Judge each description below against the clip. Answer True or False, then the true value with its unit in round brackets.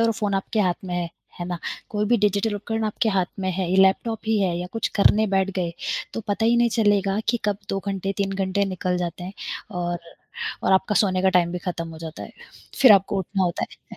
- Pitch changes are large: False (2.6 semitones)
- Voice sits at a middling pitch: False (195 Hz)